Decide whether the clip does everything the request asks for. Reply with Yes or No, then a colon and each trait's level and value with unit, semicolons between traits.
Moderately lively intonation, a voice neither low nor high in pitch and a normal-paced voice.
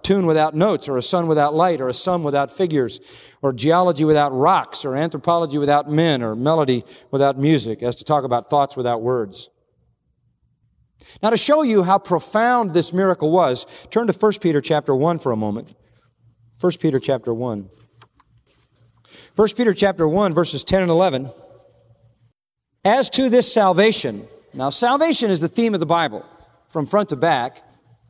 No: wide, 6.5 semitones; medium, 155 Hz; average, 165 wpm